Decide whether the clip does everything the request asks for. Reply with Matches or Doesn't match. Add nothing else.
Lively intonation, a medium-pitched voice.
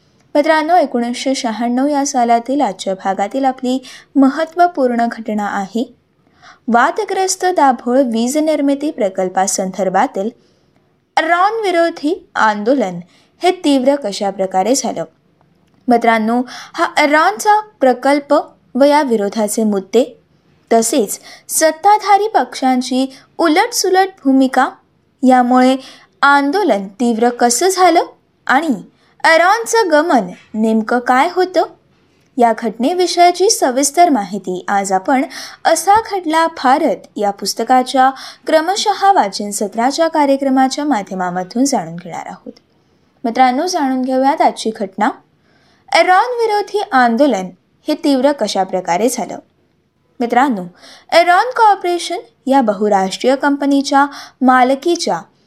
Doesn't match